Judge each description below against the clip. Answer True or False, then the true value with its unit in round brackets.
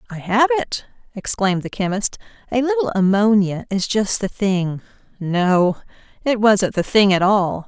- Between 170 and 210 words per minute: False (150 wpm)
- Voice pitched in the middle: False (205 Hz)